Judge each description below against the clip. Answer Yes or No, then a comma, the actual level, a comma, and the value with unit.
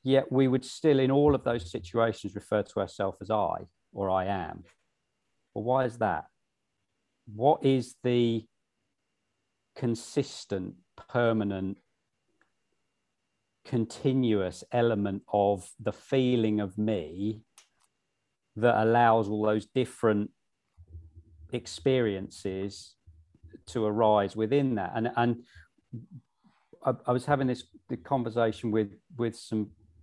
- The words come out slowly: Yes, slow, 110 wpm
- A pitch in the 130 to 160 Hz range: No, low, 110 Hz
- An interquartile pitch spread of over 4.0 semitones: No, average, 3.7 semitones